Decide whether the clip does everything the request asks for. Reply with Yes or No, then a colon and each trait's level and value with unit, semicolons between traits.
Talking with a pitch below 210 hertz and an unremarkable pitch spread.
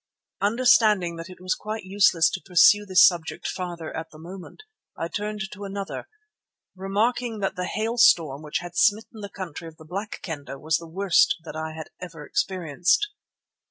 Yes: medium, 185 Hz; average, 3.8 semitones